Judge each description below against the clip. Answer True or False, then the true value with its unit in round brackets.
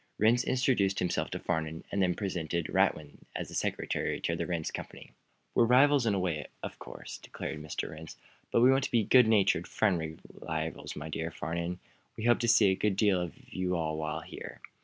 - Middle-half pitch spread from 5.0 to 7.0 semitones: True (5.6 semitones)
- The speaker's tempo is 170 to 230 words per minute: True (195 wpm)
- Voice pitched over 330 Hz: False (90 Hz)